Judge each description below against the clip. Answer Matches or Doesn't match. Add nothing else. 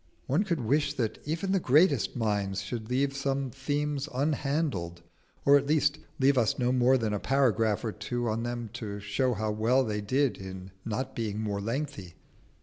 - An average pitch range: Matches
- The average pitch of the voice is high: Doesn't match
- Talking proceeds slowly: Doesn't match